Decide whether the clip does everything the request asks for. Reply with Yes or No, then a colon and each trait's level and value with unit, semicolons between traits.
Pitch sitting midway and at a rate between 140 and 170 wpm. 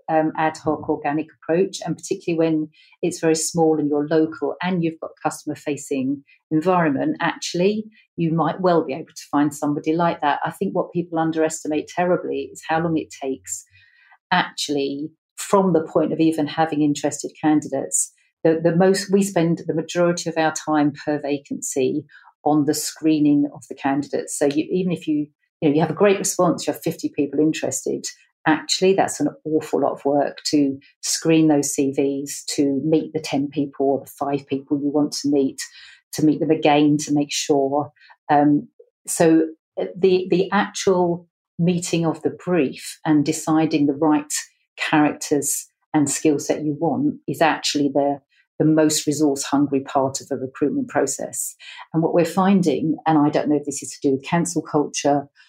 No: medium, 155 Hz; average, 180 wpm